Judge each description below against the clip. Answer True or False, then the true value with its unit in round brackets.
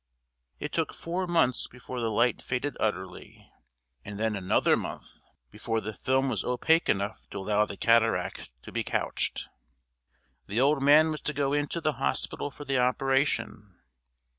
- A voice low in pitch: True (125 Hz)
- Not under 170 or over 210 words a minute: False (160 wpm)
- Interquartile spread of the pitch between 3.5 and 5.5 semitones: True (5.1 semitones)